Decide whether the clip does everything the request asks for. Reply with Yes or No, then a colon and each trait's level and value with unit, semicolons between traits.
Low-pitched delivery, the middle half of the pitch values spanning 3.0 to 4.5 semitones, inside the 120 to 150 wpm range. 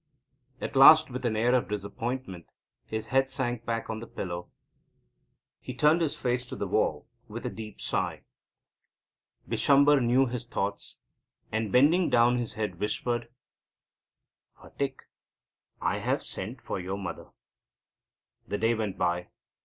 Yes: low, 120 Hz; average, 3.8 semitones; average, 140 wpm